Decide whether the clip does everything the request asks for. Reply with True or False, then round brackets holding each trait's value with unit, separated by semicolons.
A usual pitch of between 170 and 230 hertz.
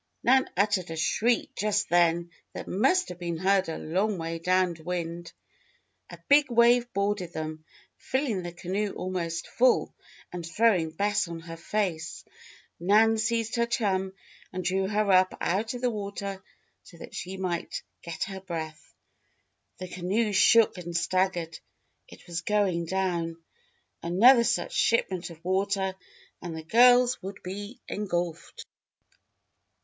True (190 Hz)